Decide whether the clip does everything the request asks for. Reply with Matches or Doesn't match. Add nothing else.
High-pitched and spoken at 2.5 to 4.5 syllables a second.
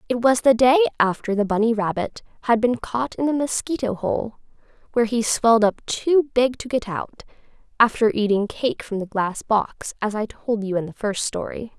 Doesn't match